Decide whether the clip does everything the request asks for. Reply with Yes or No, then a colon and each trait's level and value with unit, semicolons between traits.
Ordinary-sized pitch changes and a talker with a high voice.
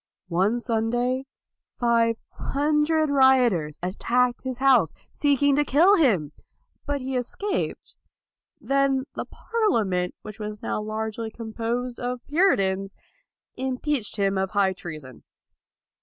Yes: average, 4.7 semitones; high, 240 Hz